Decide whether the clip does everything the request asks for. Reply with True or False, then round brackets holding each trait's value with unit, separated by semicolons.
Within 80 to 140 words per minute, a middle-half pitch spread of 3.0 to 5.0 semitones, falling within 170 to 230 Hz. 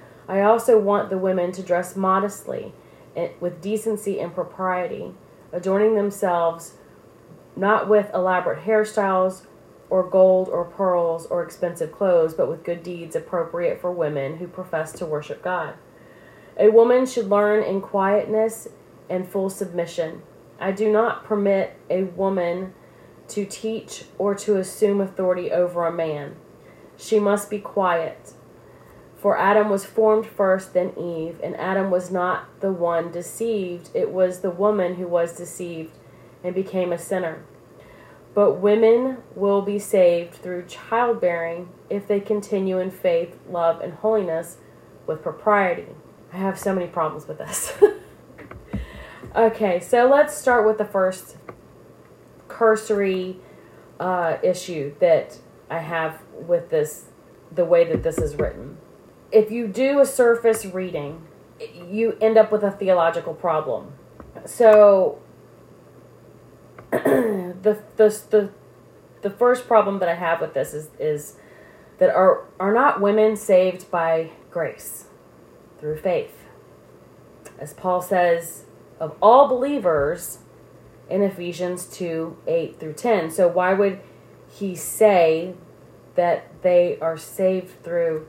True (135 wpm; 3.6 semitones; 190 Hz)